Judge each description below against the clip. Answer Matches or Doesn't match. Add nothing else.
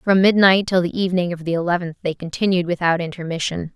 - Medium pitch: Matches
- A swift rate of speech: Doesn't match